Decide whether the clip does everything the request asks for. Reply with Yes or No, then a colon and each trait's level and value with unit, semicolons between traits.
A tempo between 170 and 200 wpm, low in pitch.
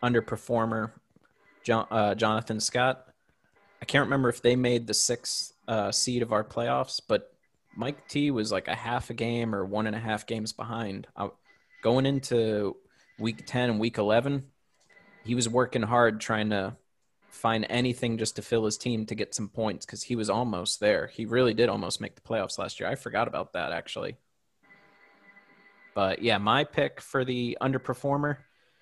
Yes: average, 175 wpm; low, 115 Hz